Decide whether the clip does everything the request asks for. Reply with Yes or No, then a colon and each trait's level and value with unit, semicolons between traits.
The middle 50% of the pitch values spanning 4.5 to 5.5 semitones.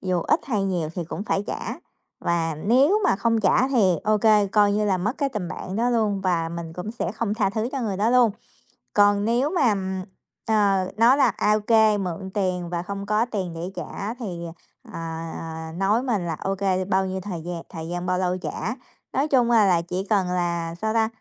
No: average, 3.8 semitones